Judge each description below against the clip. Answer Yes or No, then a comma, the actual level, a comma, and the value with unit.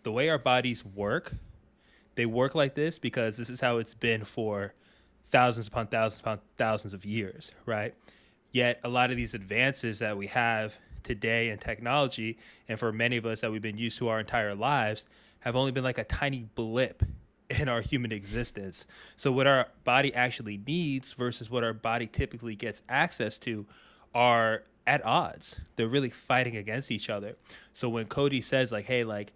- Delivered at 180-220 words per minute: Yes, average, 185 wpm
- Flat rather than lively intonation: Yes, narrow, 2.3 semitones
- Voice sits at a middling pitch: No, low, 115 Hz